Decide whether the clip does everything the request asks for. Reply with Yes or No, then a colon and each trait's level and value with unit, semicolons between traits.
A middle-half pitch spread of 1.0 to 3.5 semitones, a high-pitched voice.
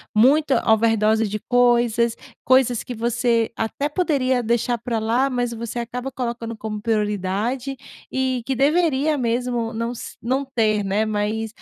Yes: narrow, 2.6 semitones; high, 235 Hz